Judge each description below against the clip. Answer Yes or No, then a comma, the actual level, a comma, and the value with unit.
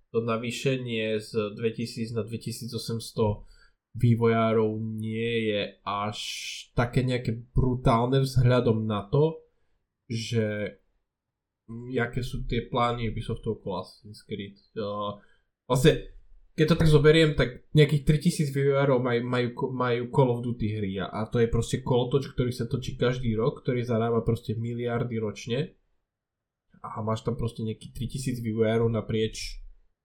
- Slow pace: No, average, 130 wpm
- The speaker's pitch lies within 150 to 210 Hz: No, low, 115 Hz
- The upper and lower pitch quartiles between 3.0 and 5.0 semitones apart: No, narrow, 2.5 semitones